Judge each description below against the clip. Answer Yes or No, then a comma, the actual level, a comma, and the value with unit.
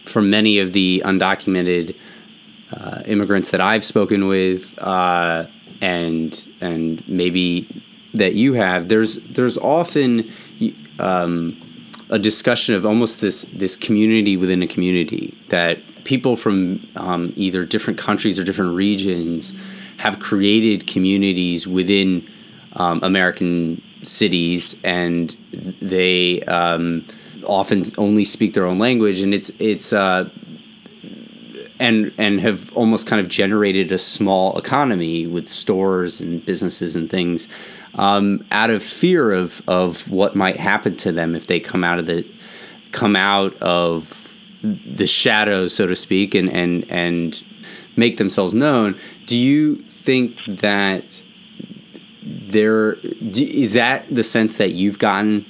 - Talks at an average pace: No, slow, 130 wpm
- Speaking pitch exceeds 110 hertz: No, very low, 95 Hz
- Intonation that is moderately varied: Yes, average, 3.6 semitones